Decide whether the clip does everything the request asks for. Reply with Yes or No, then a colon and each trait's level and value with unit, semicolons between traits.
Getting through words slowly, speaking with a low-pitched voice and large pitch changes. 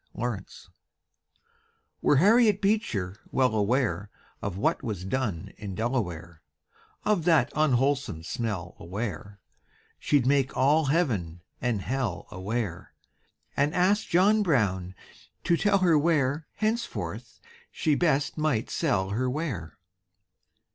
Yes: slow, 115 wpm; low, 130 Hz; wide, 7.9 semitones